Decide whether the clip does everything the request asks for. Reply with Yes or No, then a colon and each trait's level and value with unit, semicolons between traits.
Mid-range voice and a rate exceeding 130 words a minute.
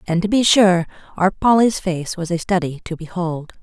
Yes: medium, 180 Hz; average, 200 wpm